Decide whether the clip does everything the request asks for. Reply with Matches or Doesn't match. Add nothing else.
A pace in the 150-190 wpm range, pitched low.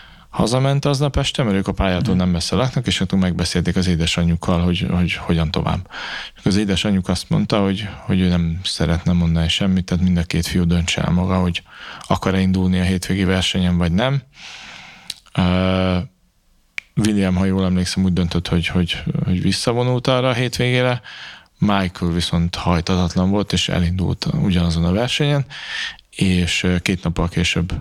Matches